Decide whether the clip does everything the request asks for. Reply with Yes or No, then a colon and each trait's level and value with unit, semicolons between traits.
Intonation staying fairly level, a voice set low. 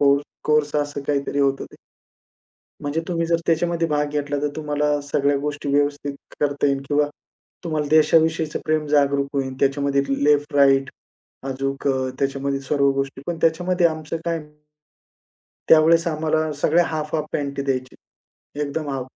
No: narrow, 2.1 semitones; medium, 145 Hz